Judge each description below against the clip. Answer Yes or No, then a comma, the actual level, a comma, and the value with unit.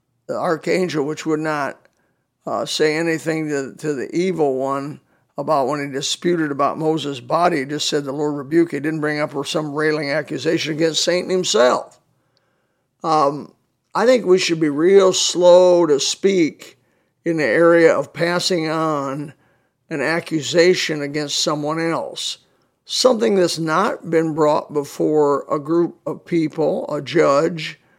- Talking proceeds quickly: No, average, 150 wpm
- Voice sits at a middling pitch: Yes, medium, 160 Hz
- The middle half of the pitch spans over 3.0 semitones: No, narrow, 2.6 semitones